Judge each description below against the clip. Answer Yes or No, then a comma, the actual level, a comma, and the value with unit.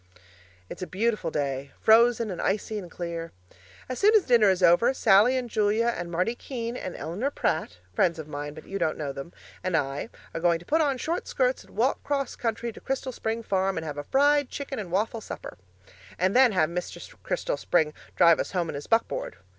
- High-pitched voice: Yes, high, 200 Hz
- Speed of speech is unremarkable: No, fast, 210 wpm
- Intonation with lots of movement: Yes, wide, 6.4 semitones